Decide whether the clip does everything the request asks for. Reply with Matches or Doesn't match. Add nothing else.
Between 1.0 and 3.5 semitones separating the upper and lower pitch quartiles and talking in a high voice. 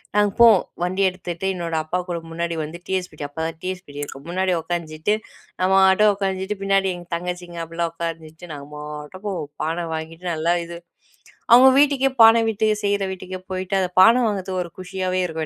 Doesn't match